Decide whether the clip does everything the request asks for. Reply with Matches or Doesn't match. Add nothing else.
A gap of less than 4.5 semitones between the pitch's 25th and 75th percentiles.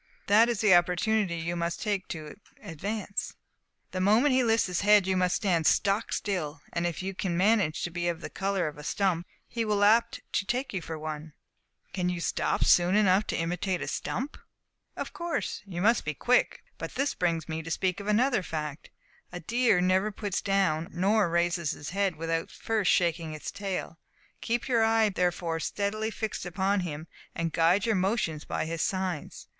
Matches